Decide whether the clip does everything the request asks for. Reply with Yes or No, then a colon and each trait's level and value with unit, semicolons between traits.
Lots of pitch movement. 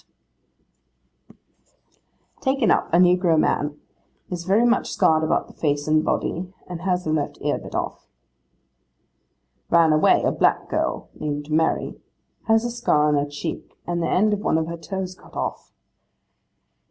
No: average, 3.5 semitones